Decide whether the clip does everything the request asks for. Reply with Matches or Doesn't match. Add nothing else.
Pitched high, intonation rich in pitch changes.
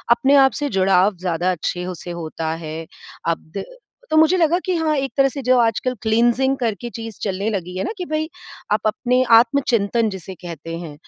Matches